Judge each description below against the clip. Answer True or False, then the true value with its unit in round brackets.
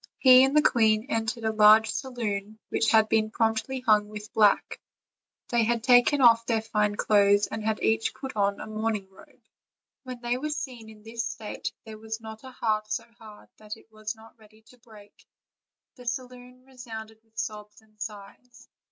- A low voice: False (220 Hz)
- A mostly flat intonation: True (2.0 semitones)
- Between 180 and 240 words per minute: True (185 wpm)